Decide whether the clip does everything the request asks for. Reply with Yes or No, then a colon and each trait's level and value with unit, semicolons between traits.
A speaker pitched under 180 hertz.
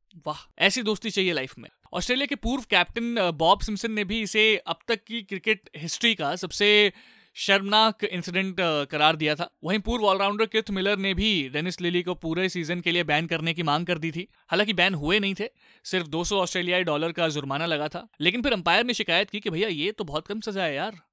No: high, 190 Hz